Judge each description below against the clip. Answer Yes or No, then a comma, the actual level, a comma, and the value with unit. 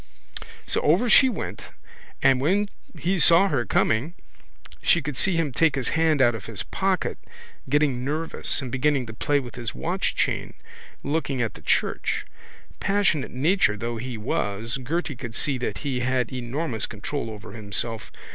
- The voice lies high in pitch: No, low, 135 Hz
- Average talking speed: Yes, average, 165 wpm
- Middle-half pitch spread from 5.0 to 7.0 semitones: Yes, average, 5.3 semitones